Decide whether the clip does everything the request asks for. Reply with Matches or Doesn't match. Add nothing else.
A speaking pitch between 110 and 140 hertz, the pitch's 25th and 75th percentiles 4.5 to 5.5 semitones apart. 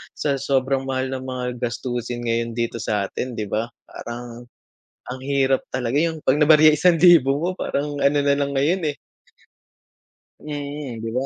Doesn't match